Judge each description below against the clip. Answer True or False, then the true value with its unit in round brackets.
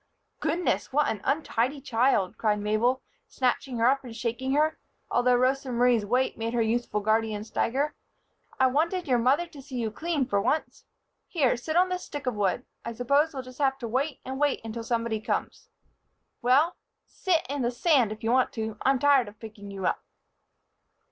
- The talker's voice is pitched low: False (250 Hz)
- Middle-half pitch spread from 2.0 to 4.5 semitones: True (3.8 semitones)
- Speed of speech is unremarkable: True (190 wpm)